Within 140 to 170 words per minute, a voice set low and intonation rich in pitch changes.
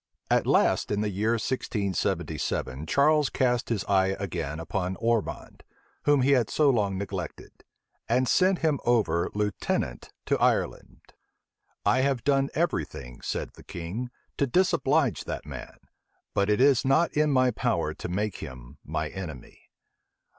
Yes: average, 145 wpm; low, 110 Hz; wide, 6.5 semitones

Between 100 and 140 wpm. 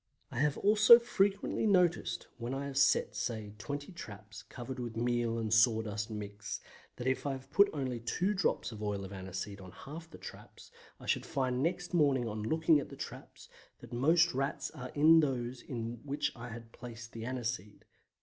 No: average, 190 wpm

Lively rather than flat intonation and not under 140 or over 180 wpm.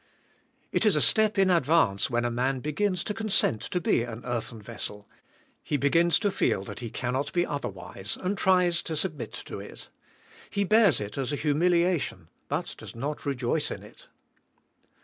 Yes: wide, 7.1 semitones; average, 175 wpm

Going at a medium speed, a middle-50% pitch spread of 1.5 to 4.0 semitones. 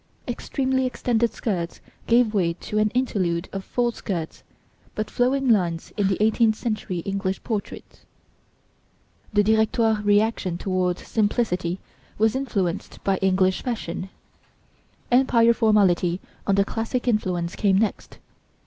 No: slow, 120 wpm; average, 3.7 semitones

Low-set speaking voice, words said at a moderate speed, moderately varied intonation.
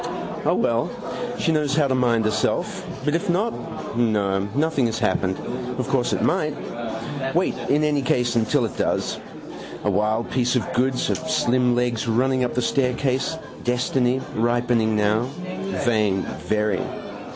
Yes: low, 120 Hz; average, 150 wpm; average, 3.3 semitones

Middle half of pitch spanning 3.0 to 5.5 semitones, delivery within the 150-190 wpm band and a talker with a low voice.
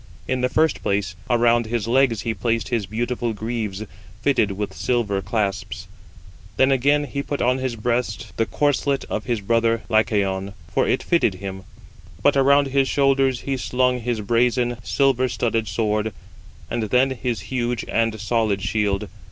Yes: average, 3.4 semitones; average, 160 wpm; low, 115 Hz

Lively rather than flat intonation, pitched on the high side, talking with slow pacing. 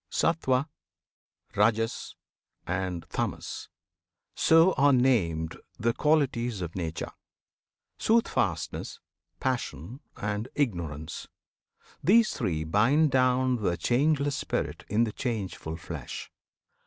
No: wide, 7.4 semitones; low, 115 Hz; slow, 95 wpm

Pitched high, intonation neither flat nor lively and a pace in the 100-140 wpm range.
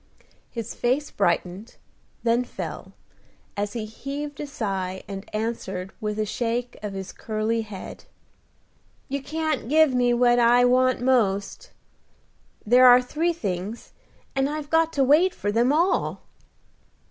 Yes: high, 240 Hz; average, 4.7 semitones; slow, 135 wpm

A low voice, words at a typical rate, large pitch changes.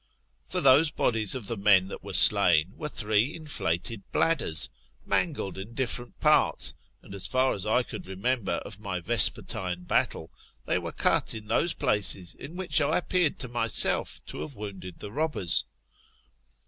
Yes: low, 110 Hz; average, 155 wpm; wide, 6.0 semitones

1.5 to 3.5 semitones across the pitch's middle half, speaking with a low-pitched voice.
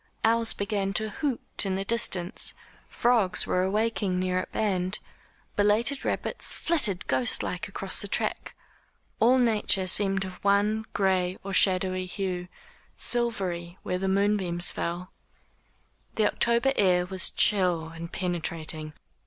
No: average, 2.8 semitones; high, 195 Hz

